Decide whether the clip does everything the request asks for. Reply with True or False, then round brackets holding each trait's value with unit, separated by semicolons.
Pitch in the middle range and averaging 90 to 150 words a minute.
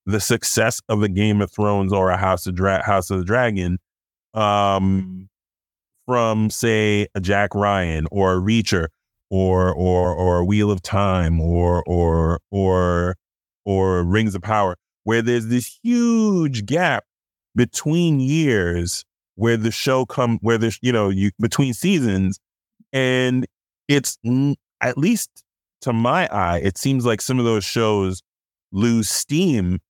False (105 Hz; 145 wpm)